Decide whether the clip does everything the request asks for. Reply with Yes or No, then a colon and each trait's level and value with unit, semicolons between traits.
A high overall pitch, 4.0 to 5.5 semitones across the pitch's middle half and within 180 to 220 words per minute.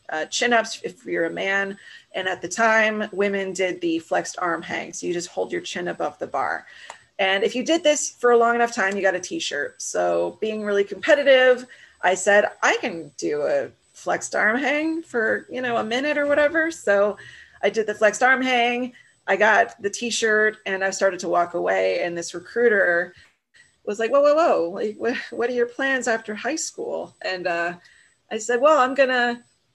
Yes: high, 220 Hz; average, 4.8 semitones; average, 200 wpm